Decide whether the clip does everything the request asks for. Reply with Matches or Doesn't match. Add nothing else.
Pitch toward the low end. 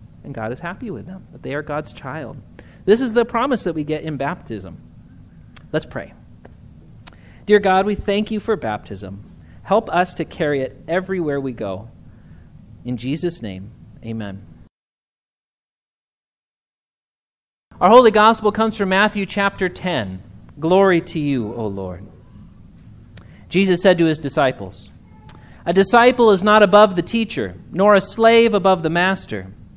Doesn't match